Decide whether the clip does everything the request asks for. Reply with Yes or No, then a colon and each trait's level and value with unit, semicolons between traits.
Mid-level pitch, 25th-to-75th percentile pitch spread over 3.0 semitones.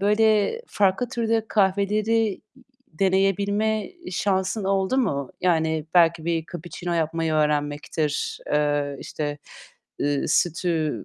Yes: medium, 180 Hz; average, 4.6 semitones